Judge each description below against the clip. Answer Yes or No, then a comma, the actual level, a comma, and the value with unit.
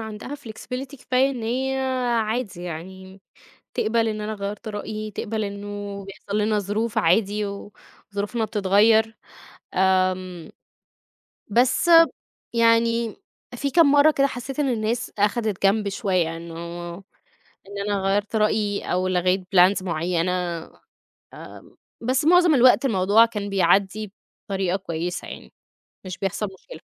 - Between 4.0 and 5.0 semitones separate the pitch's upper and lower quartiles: No, average, 3.3 semitones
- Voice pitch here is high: Yes, high, 210 Hz